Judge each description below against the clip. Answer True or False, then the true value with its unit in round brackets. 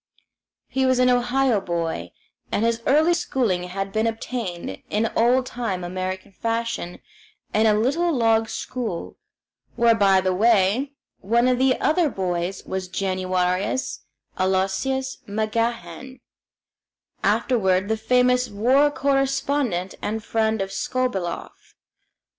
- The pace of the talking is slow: True (120 wpm)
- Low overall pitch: False (225 Hz)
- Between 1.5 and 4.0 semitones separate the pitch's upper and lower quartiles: False (5.0 semitones)